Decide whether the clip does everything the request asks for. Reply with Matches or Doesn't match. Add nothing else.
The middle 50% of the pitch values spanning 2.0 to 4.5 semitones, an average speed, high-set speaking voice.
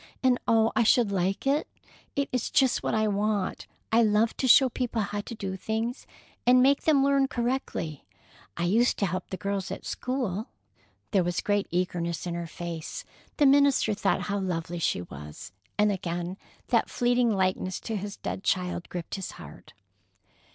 Doesn't match